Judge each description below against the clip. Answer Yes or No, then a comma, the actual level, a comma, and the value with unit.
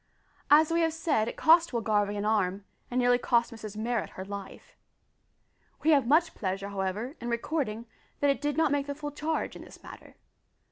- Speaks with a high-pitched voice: Yes, high, 245 Hz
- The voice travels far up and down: Yes, wide, 5.8 semitones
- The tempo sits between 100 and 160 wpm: No, average, 195 wpm